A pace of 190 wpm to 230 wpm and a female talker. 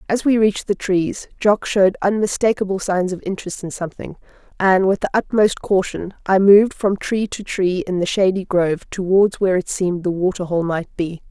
Yes: average, 195 wpm; female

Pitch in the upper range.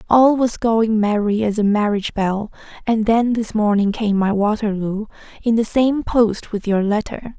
Yes: high, 215 Hz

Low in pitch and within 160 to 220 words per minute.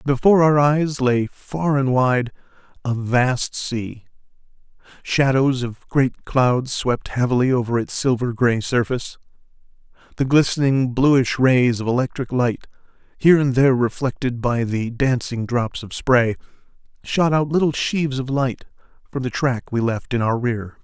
No: low, 130 Hz; average, 150 wpm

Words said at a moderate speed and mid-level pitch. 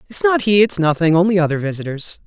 No: fast, 210 wpm; medium, 165 Hz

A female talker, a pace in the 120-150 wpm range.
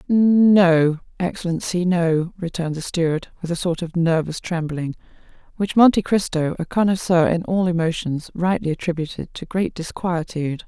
Yes: female; average, 140 wpm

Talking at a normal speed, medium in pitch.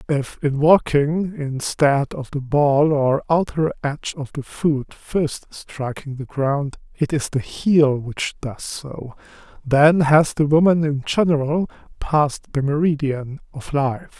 Yes: average, 150 wpm; medium, 145 Hz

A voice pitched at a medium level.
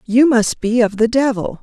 No: high, 230 Hz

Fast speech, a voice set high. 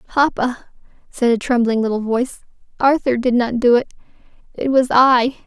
No: average, 155 wpm; high, 245 Hz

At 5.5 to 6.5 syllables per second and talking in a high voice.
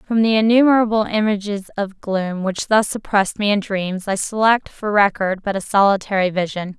No: 5.2 syllables/s; high, 205 Hz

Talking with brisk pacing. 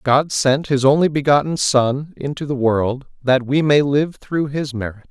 No: average, 190 wpm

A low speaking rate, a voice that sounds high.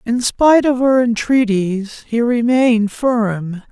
Yes: slow, 130 wpm; high, 230 Hz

